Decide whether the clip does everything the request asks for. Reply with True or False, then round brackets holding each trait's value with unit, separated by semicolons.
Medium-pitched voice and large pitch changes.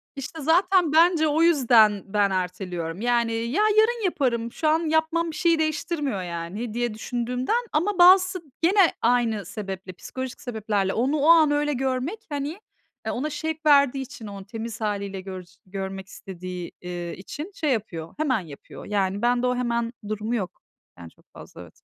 False (245 Hz; 7.7 semitones)